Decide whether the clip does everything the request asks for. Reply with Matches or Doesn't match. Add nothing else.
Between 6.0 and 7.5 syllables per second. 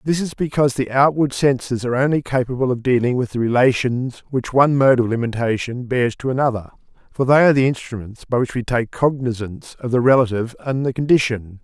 Matches